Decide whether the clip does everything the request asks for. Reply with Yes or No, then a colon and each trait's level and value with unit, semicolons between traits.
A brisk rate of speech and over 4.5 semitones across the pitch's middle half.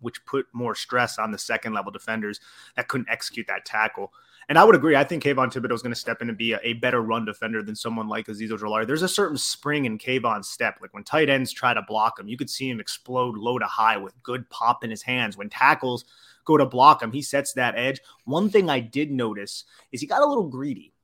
No: fast, 255 wpm; average, 3.4 semitones